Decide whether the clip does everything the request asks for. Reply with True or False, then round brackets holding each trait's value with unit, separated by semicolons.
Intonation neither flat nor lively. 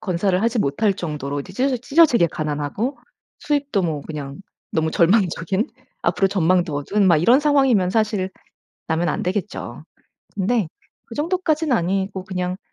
False (5.8 semitones)